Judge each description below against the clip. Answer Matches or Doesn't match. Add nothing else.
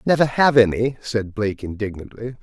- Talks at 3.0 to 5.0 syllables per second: Doesn't match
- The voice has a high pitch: Doesn't match